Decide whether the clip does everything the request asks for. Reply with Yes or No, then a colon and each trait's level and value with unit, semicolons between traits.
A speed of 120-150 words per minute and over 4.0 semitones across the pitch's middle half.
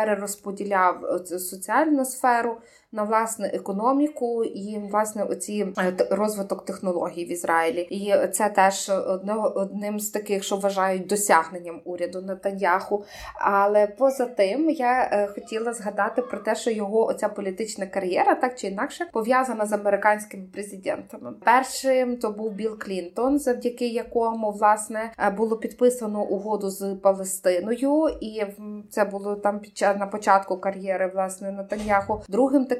No: average, 130 wpm; average, 2.8 semitones